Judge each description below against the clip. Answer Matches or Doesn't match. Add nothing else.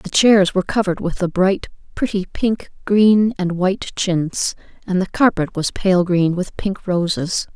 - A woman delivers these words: Matches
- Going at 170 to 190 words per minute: Matches